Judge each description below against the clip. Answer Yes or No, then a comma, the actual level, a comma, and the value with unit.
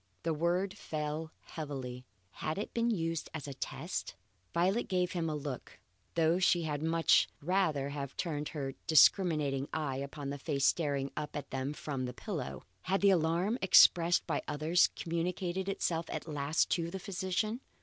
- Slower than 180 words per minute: Yes, average, 165 wpm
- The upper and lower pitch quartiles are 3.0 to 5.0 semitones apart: Yes, average, 3.7 semitones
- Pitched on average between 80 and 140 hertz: No, medium, 160 Hz